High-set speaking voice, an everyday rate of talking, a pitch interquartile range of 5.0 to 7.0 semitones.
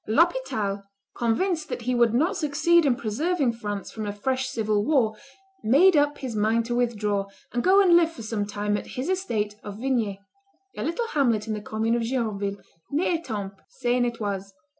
Yes: high, 235 Hz; average, 185 wpm; wide, 5.6 semitones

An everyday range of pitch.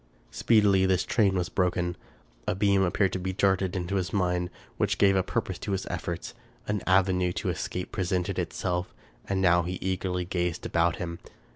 No: narrow, 1.4 semitones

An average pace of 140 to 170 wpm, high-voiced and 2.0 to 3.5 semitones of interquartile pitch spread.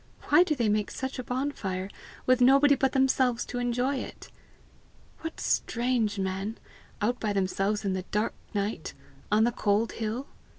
No: average, 160 wpm; high, 230 Hz; average, 3.9 semitones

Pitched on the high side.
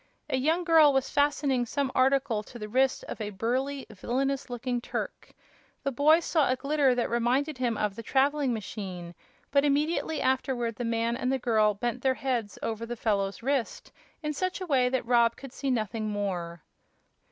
Yes: very high, 250 Hz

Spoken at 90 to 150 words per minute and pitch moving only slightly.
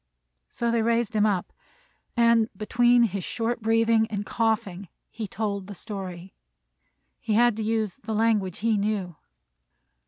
Yes: average, 145 wpm; narrow, 2.3 semitones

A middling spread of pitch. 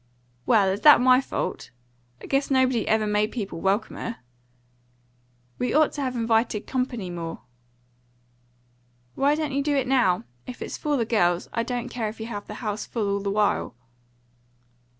Yes: average, 3.9 semitones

